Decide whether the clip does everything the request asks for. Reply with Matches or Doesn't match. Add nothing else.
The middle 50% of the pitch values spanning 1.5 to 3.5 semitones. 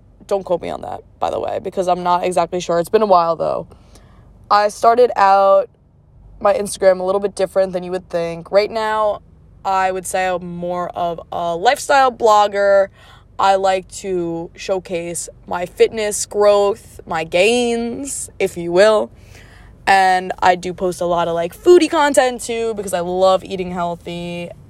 Matches